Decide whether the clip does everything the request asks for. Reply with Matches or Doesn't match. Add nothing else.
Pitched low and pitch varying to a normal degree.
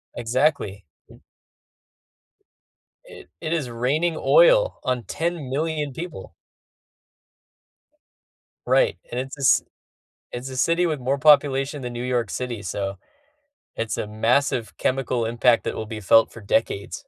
Matches